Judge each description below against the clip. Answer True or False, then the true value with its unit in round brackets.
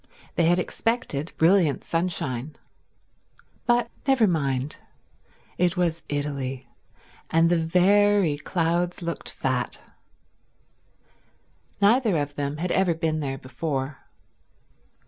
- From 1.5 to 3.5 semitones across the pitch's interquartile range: False (4.0 semitones)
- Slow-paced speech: True (100 wpm)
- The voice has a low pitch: False (165 Hz)